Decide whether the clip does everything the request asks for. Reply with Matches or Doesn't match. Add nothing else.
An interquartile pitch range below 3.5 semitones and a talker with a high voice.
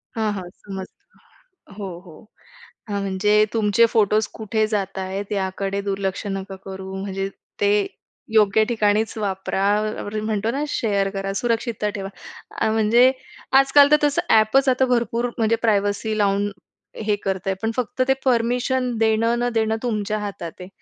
Matches